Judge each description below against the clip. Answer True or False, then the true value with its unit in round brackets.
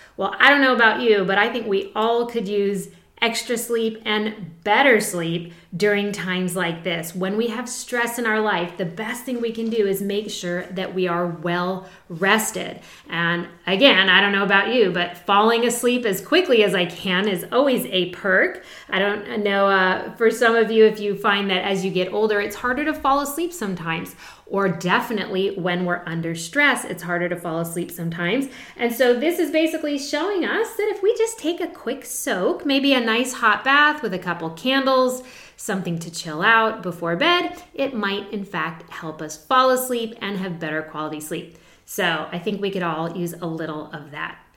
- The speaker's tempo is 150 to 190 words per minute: False (200 wpm)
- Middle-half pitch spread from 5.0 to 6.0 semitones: True (5.3 semitones)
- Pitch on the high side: True (205 Hz)